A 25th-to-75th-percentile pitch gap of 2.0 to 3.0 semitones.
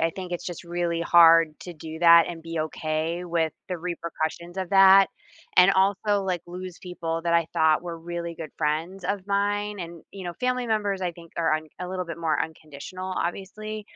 Yes: narrow, 2.4 semitones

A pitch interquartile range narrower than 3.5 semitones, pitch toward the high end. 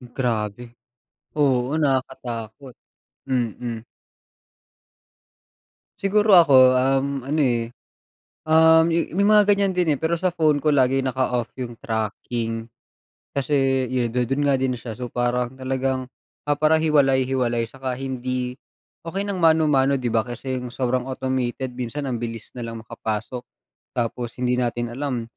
No: average, 3.0 semitones; low, 130 Hz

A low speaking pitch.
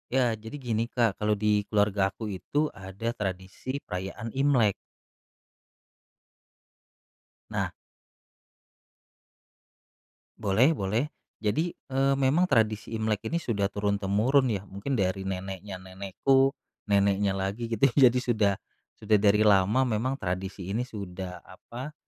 Yes: low, 105 Hz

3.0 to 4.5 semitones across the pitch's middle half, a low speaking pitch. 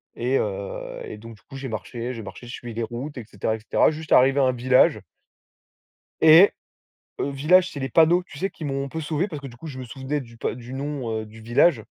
Yes: average, 4.2 semitones; low, 130 Hz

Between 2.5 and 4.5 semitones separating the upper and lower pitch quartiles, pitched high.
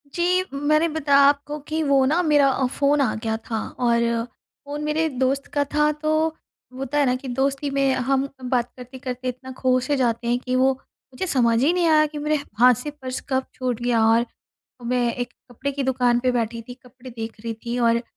Yes: average, 3.0 semitones; very high, 260 Hz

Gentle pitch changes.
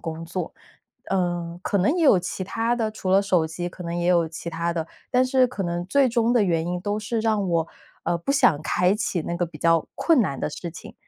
No: average, 4.3 semitones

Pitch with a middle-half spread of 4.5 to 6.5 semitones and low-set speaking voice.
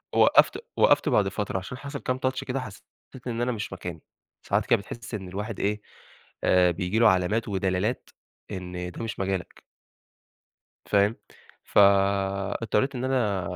No: average, 3.6 semitones; low, 100 Hz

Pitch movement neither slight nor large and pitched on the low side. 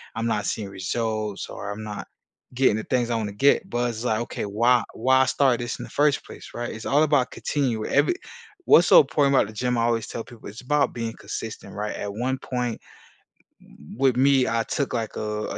Yes: average, 3.2 semitones; low, 120 Hz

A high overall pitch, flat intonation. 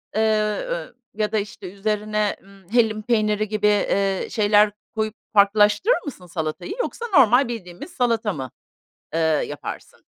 Yes: high, 210 Hz; narrow, 2.0 semitones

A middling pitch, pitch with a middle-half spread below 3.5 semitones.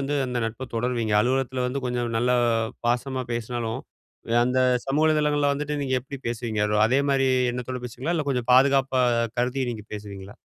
No: low, 125 Hz; narrow, 2.4 semitones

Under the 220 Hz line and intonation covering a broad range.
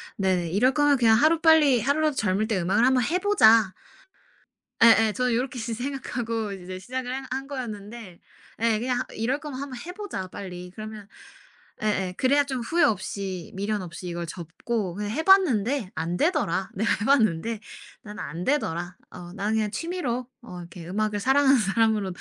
No: high, 225 Hz; wide, 5.7 semitones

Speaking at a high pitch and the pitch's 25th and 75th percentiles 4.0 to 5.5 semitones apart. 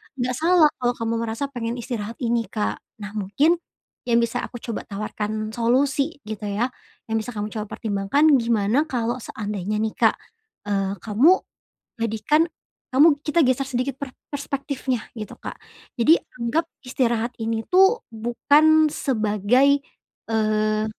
Yes: high, 235 Hz; average, 4.4 semitones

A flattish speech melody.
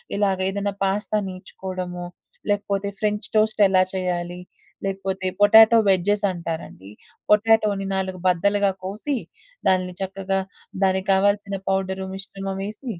Yes: narrow, 1.5 semitones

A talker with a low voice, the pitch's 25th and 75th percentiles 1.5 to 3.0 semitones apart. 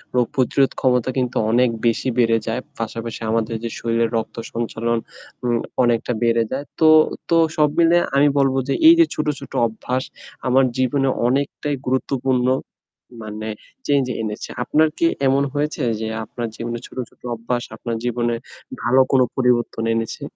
Yes: low, 125 Hz; narrow, 2.6 semitones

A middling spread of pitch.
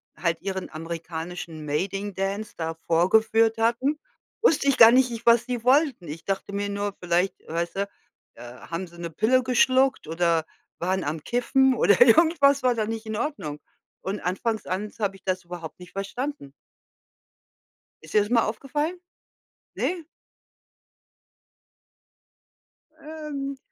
No: wide, 6.4 semitones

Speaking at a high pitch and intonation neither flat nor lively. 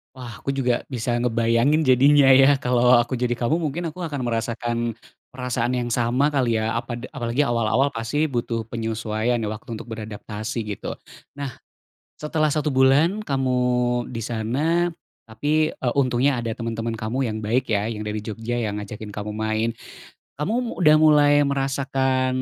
No: low, 120 Hz; average, 3.4 semitones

